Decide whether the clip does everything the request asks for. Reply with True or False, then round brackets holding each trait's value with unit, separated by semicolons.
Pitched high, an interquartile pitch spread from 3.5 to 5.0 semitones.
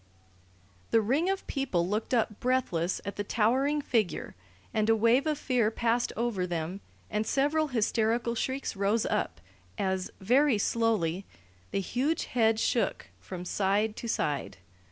True (225 Hz; 4.2 semitones)